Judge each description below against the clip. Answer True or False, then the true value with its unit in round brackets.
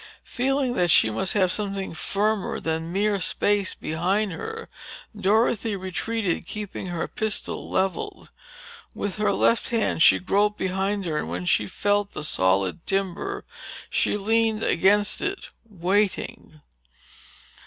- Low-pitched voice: False (195 Hz)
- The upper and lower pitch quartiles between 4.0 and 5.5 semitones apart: False (3.2 semitones)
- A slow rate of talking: True (130 wpm)